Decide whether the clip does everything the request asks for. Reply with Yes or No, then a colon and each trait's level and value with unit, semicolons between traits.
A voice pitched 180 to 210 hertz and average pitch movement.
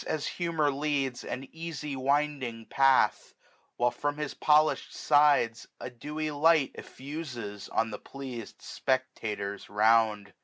No: low, 135 Hz; average, 4.5 semitones